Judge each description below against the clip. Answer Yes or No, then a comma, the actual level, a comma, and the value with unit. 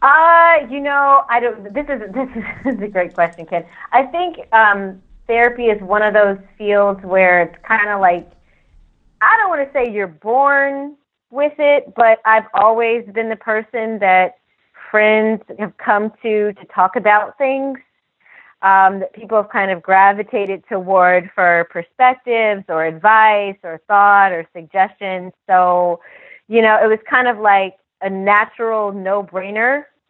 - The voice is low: No, high, 210 Hz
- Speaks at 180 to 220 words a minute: No, average, 155 wpm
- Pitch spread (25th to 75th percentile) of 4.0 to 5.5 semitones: No, average, 3.6 semitones